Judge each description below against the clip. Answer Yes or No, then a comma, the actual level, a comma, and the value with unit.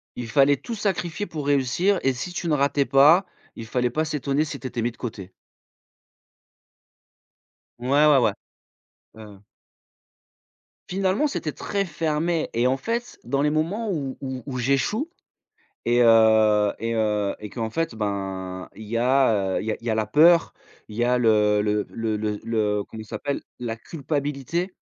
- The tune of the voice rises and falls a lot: Yes, wide, 5.8 semitones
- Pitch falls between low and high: No, low, 130 Hz